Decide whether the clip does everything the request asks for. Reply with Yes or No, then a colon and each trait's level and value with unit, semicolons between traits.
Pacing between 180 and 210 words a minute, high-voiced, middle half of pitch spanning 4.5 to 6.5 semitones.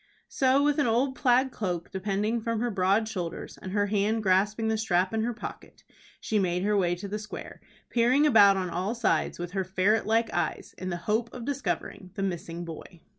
No: fast, 205 wpm; high, 210 Hz; average, 3.8 semitones